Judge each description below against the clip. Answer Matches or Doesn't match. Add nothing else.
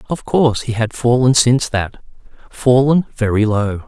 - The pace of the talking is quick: Doesn't match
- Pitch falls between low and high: Doesn't match